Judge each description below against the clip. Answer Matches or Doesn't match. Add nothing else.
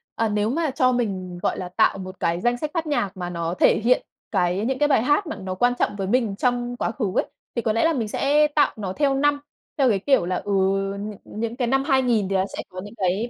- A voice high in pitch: Matches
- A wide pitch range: Matches